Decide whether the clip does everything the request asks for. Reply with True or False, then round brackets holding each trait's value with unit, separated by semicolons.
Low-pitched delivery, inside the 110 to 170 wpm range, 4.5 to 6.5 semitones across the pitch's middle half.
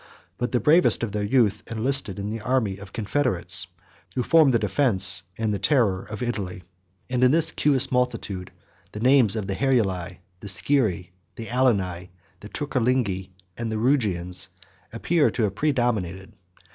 True (110 Hz; 160 wpm; 5.0 semitones)